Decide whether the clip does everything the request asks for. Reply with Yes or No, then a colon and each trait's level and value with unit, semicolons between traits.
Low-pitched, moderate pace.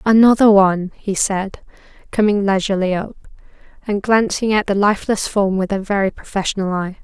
No: high, 200 Hz; average, 155 wpm